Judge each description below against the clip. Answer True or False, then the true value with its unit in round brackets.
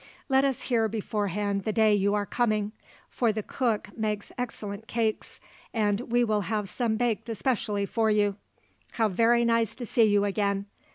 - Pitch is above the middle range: True (215 Hz)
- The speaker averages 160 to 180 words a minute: True (170 wpm)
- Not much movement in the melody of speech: True (2.2 semitones)